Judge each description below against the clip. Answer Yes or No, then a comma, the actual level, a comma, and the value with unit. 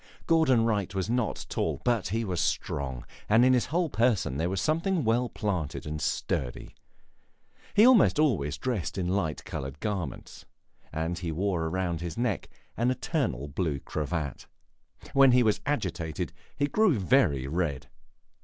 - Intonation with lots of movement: Yes, wide, 7.7 semitones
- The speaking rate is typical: Yes, average, 155 wpm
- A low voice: Yes, very low, 95 Hz